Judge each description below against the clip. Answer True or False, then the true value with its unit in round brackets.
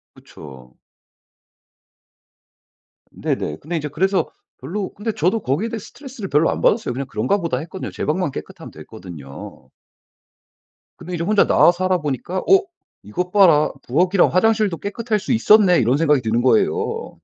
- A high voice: False (180 Hz)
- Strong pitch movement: True (6.9 semitones)